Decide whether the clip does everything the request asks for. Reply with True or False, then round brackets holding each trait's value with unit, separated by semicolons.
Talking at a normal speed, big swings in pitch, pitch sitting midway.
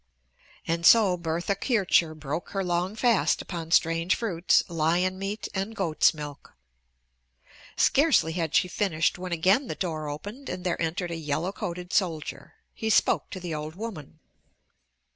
False (150 wpm; 3.3 semitones; 175 Hz)